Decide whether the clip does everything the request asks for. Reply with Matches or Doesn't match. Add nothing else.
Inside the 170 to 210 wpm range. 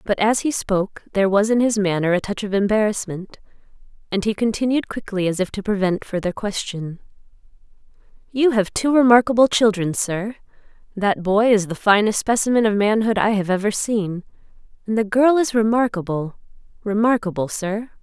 Doesn't match